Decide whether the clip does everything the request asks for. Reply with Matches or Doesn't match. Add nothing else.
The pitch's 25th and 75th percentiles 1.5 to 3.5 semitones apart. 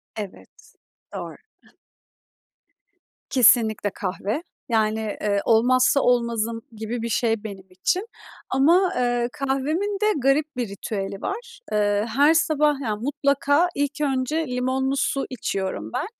Doesn't match